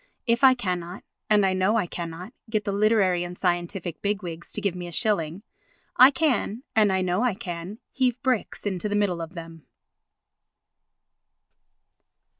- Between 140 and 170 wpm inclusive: Yes, average, 165 wpm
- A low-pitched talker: No, high, 195 Hz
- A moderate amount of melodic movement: Yes, average, 3.5 semitones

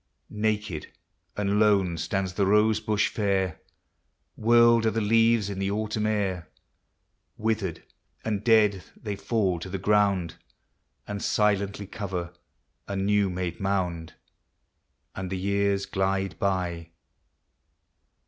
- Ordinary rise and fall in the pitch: No, narrow, 2.1 semitones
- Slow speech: Yes, slow, 120 wpm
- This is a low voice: Yes, low, 100 Hz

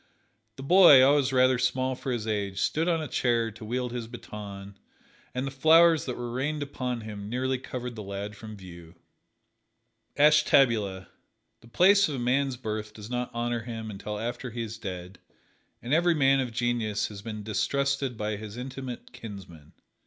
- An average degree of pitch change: Yes, average, 4.0 semitones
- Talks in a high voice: No, low, 120 Hz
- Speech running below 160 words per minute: No, average, 175 wpm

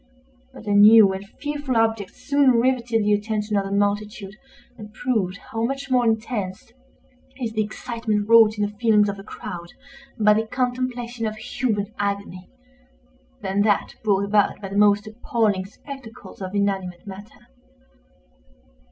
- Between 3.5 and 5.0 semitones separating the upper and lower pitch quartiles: No, narrow, 2.5 semitones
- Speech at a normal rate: Yes, average, 150 wpm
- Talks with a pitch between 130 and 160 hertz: No, high, 215 Hz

